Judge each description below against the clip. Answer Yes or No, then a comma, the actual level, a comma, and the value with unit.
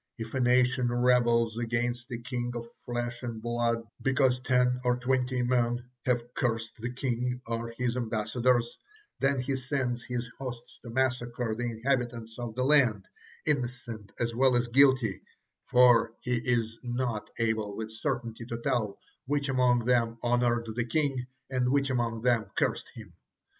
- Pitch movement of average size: No, narrow, 1.4 semitones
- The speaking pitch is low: Yes, low, 120 Hz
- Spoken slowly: No, average, 155 wpm